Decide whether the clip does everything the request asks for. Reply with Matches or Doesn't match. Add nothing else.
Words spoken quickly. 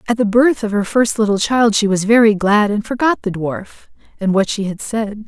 Matches